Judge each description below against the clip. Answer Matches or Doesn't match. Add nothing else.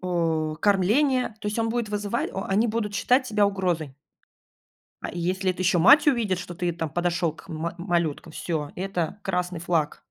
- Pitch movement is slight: Doesn't match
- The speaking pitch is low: Doesn't match